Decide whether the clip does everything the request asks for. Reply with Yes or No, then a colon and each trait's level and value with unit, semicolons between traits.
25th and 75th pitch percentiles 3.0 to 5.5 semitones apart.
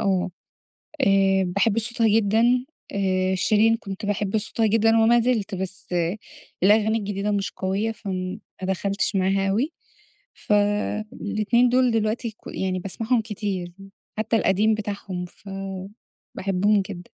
No: narrow, 2.4 semitones